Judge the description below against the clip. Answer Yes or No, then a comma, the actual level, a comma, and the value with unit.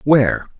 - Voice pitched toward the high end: No, low, 130 Hz